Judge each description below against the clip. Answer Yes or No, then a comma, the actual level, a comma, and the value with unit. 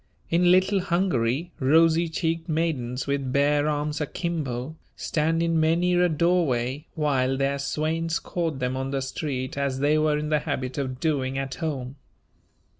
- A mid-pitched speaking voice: Yes, medium, 150 Hz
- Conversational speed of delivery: Yes, average, 155 wpm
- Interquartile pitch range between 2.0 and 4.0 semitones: Yes, average, 3.6 semitones